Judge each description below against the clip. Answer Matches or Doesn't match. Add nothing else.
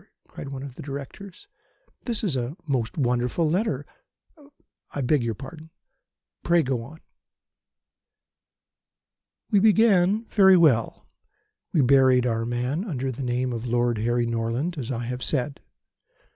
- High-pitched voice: Doesn't match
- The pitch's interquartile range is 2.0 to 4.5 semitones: Doesn't match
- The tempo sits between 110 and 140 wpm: Matches